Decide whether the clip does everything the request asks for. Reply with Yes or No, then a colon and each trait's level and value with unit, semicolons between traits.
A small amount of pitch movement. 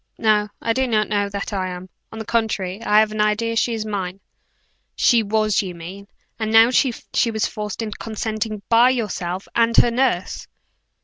Yes: narrow, 2.2 semitones